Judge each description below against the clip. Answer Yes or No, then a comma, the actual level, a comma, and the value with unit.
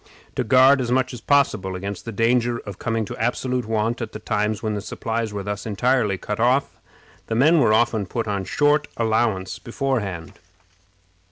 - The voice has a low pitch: Yes, low, 115 Hz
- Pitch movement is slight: No, average, 3.3 semitones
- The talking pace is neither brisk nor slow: Yes, average, 180 wpm